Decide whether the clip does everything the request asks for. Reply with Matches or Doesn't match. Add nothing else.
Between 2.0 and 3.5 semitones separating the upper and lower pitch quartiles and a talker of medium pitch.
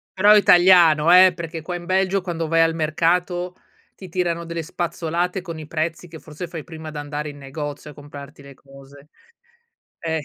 Matches